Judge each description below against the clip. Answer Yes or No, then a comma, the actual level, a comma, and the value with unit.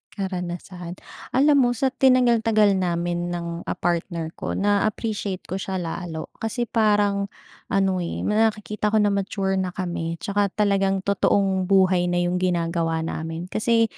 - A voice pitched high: Yes, high, 195 Hz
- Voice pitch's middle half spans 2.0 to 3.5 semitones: Yes, average, 3.2 semitones